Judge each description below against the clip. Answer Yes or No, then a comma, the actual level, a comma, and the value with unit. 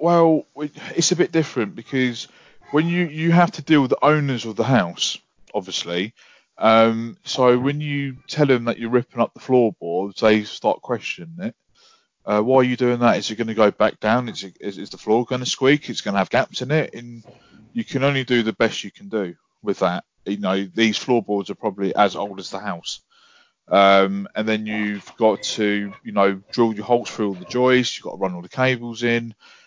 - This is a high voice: No, low, 120 Hz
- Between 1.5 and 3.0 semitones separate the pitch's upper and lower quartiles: No, average, 4.9 semitones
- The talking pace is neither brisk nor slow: No, fast, 220 wpm